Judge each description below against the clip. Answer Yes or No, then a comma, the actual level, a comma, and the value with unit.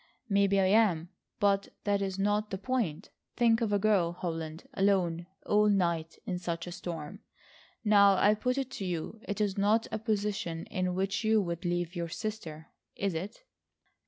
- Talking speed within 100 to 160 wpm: No, average, 175 wpm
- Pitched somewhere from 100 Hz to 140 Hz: No, high, 195 Hz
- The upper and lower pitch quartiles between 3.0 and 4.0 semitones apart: Yes, average, 3.4 semitones